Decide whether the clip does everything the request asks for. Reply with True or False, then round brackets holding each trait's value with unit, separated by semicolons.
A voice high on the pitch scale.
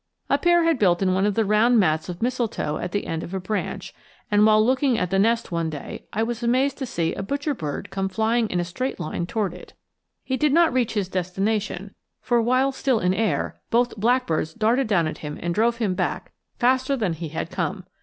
True (215 Hz)